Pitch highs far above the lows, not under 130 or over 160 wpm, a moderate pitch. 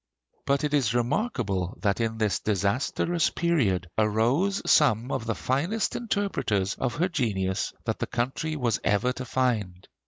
No: wide, 6.2 semitones; average, 150 wpm; low, 120 Hz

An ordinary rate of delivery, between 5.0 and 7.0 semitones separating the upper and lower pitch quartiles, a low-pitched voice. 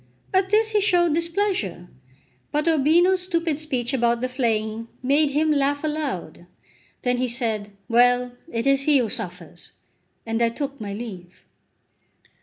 No: average, 145 wpm; average, 5.3 semitones; very high, 270 Hz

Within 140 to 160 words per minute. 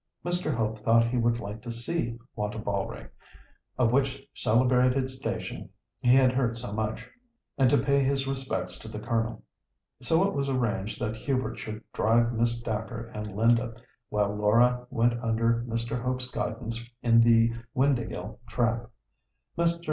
Yes: average, 150 wpm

